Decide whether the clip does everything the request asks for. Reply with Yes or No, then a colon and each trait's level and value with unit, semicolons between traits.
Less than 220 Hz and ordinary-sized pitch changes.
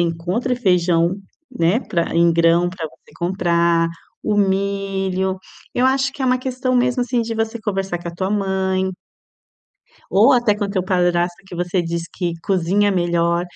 Yes: high, 190 Hz; average, 3.8 semitones